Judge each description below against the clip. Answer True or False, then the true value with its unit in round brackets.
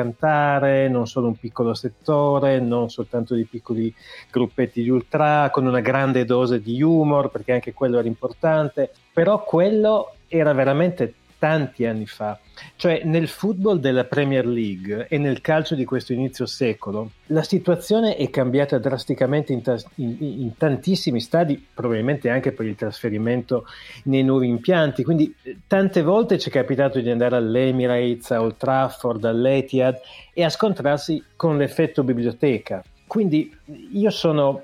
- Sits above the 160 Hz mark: False (135 Hz)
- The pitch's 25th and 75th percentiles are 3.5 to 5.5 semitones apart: True (4.3 semitones)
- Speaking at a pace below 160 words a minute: True (150 wpm)